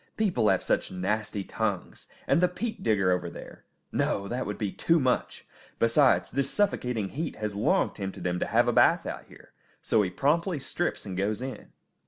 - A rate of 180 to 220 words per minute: Yes, average, 190 wpm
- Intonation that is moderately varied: No, wide, 6.7 semitones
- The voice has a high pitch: No, low, 110 Hz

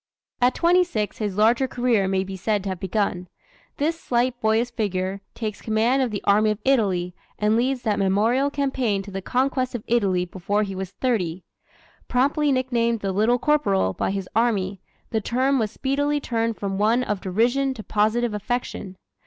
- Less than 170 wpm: No, average, 180 wpm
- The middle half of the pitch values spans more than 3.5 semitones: Yes, average, 4.2 semitones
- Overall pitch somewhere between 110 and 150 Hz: No, high, 220 Hz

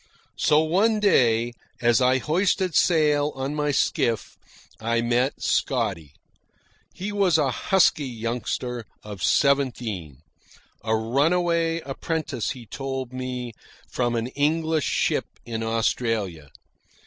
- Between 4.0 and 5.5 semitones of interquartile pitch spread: Yes, average, 5.1 semitones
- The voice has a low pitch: Yes, low, 130 Hz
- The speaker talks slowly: Yes, slow, 110 wpm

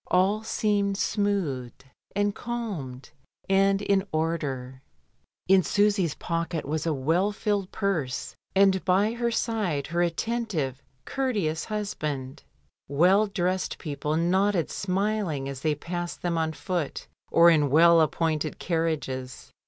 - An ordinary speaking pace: No, slow, 125 wpm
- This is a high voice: No, medium, 175 Hz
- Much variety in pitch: No, average, 4.7 semitones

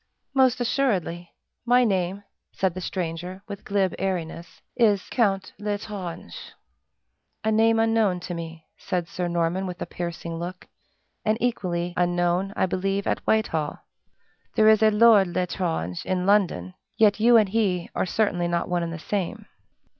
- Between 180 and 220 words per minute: No, average, 150 wpm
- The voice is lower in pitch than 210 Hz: Yes, medium, 185 Hz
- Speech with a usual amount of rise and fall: Yes, average, 3.7 semitones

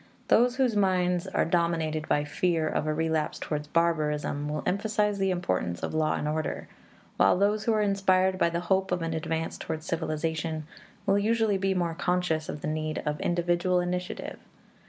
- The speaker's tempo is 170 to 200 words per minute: Yes, average, 175 wpm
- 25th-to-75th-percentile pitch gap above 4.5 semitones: No, average, 3.3 semitones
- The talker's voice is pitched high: No, medium, 170 Hz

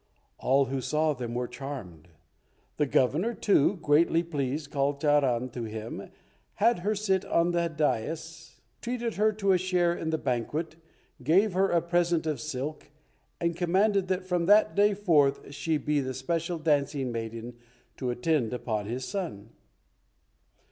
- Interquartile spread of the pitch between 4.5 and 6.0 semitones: Yes, average, 5.2 semitones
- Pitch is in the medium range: Yes, medium, 155 Hz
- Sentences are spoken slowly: No, average, 155 wpm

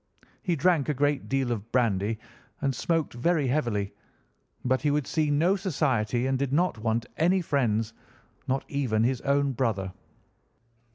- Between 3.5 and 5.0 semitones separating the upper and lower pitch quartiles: Yes, average, 4.3 semitones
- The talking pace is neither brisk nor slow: Yes, average, 155 wpm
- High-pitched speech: No, low, 135 Hz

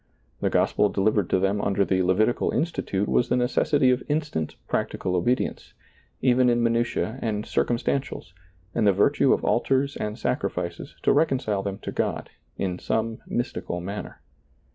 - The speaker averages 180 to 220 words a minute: No, average, 160 wpm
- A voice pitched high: No, low, 110 Hz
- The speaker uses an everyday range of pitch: Yes, average, 4.4 semitones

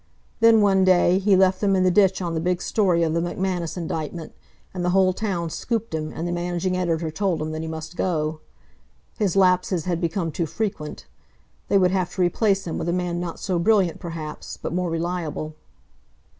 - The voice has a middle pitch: Yes, medium, 175 Hz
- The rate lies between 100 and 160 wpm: No, average, 200 wpm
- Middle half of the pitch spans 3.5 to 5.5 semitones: No, narrow, 2.4 semitones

